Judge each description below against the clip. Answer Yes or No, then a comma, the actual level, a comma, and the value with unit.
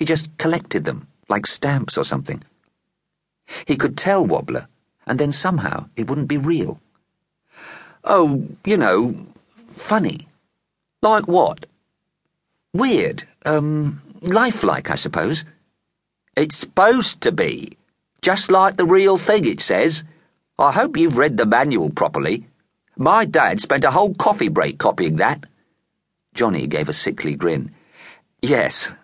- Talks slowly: Yes, slow, 130 wpm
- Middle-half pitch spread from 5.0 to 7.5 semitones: Yes, wide, 5.4 semitones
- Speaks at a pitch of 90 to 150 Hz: No, medium, 170 Hz